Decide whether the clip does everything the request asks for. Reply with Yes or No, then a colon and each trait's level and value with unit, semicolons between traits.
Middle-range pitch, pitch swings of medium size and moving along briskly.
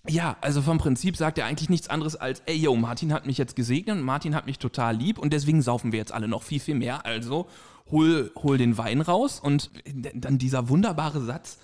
Yes: medium, 145 Hz; average, 3.7 semitones; fast, 225 wpm